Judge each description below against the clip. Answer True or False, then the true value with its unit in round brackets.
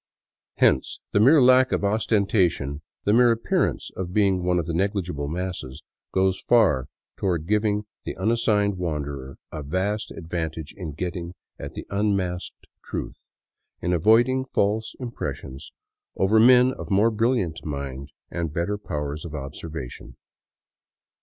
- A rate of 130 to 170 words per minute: True (140 wpm)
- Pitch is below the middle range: True (95 Hz)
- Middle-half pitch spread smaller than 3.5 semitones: False (5.4 semitones)